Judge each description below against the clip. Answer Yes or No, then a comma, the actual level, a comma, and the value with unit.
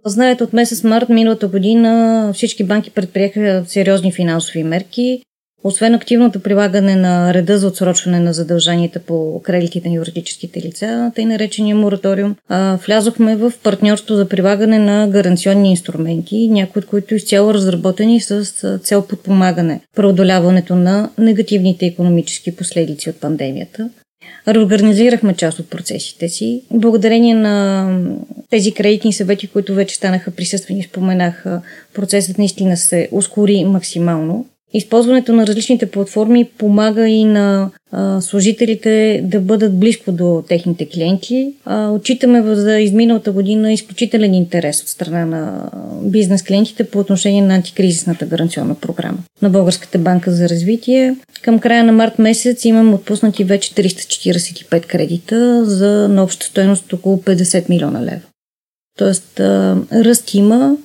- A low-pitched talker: No, high, 200 Hz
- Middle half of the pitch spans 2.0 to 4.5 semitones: Yes, average, 3.4 semitones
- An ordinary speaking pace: Yes, average, 130 wpm